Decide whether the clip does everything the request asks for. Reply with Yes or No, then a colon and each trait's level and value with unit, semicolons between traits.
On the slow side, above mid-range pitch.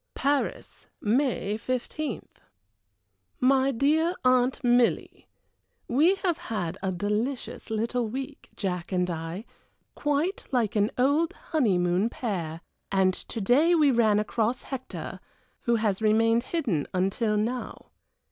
Yes: slow, 120 wpm; high, 230 Hz